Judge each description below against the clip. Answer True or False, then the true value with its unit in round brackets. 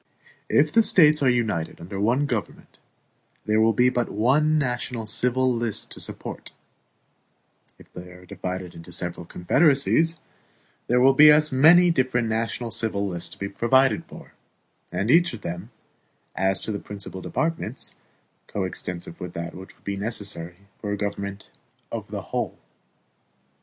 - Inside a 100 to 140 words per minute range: False (150 wpm)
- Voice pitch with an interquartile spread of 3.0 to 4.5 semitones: False (5.5 semitones)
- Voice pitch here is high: False (110 Hz)